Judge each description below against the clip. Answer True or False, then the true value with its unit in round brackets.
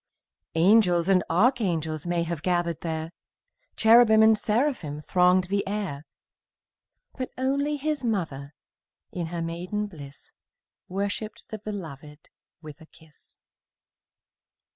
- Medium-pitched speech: True (180 Hz)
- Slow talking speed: True (110 wpm)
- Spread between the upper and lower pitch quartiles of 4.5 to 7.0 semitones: True (5.2 semitones)